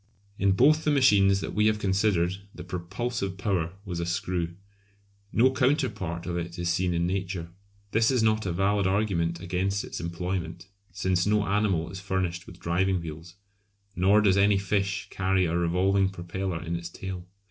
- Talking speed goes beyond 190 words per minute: No, average, 170 wpm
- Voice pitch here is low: Yes, very low, 95 Hz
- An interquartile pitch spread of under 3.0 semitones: Yes, narrow, 2.6 semitones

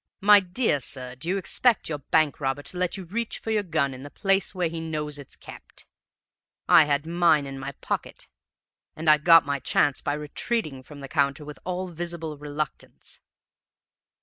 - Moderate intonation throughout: Yes, average, 3.8 semitones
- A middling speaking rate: Yes, average, 185 wpm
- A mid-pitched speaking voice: Yes, medium, 155 Hz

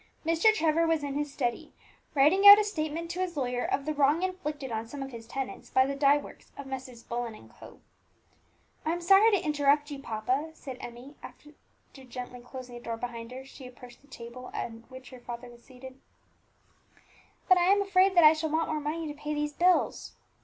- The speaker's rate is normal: No, fast, 210 wpm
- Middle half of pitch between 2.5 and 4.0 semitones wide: No, average, 4.4 semitones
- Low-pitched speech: No, very high, 285 Hz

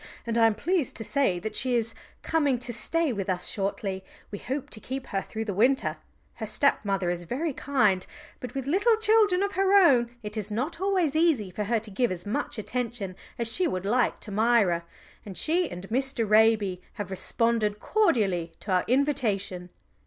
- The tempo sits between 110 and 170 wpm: No, average, 190 wpm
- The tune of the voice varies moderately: No, wide, 5.8 semitones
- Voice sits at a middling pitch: No, high, 230 Hz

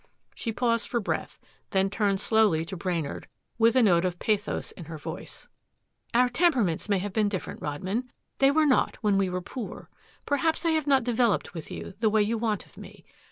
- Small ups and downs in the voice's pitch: No, average, 4.6 semitones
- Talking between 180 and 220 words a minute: Yes, average, 200 wpm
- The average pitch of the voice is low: No, high, 215 Hz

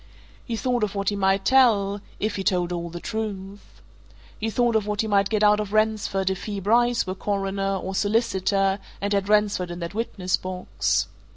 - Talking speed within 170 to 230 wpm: Yes, average, 195 wpm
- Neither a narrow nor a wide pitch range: No, narrow, 2.0 semitones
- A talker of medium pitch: No, high, 200 Hz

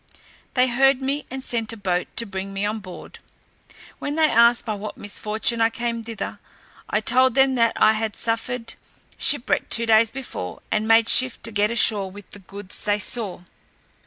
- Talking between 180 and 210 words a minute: Yes, average, 185 wpm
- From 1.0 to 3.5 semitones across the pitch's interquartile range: Yes, average, 2.8 semitones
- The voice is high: Yes, high, 225 Hz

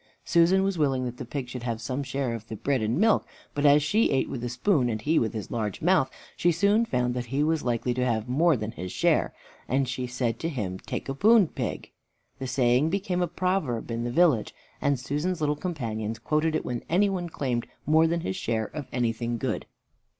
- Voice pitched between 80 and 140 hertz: Yes, low, 135 Hz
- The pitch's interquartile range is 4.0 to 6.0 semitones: Yes, wide, 5.4 semitones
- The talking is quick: Yes, fast, 225 wpm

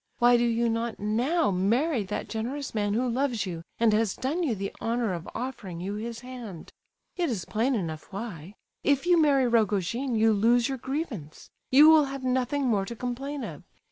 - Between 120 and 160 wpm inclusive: No, average, 190 wpm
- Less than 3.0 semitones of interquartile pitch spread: No, average, 4.1 semitones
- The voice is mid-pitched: No, high, 235 Hz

